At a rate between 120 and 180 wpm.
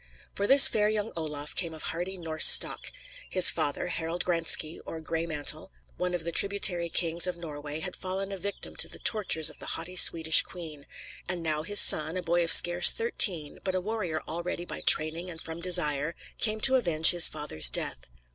No: average, 195 wpm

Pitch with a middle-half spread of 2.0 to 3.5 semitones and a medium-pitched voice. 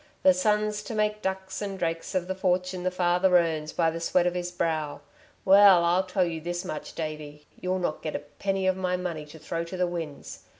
Yes: narrow, 2.4 semitones; medium, 180 Hz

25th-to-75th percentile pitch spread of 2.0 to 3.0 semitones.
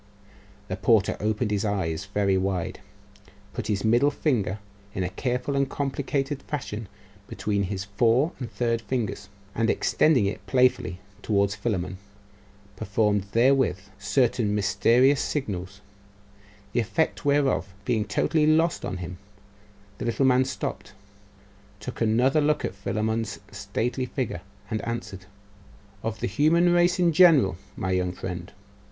No: average, 5.2 semitones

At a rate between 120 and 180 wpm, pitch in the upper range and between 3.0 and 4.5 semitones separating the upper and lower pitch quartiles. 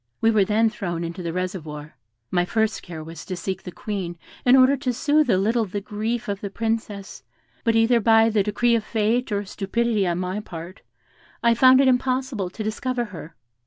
No: average, 200 wpm; high, 210 Hz; average, 4.1 semitones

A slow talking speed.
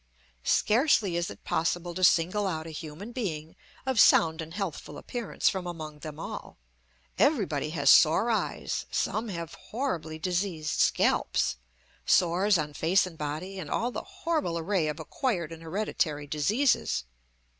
No: average, 145 wpm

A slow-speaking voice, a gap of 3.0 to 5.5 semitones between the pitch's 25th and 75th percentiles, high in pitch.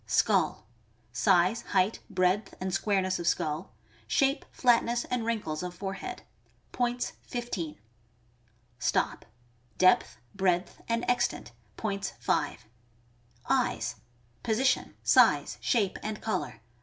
Yes: slow, 110 wpm; average, 4.5 semitones; high, 195 Hz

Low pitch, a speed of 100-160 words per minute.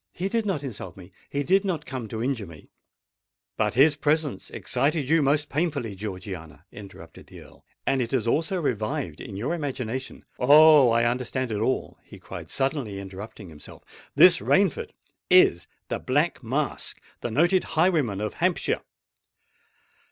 Yes: low, 130 Hz; average, 145 wpm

